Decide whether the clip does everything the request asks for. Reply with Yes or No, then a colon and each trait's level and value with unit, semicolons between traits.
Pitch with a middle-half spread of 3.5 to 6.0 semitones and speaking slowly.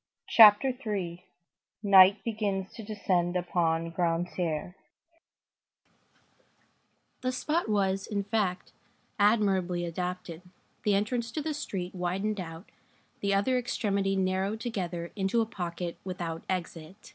No: average, 3.1 semitones; slow, 110 wpm